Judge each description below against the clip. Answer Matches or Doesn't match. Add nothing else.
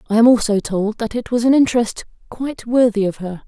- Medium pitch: Doesn't match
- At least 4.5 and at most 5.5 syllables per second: Doesn't match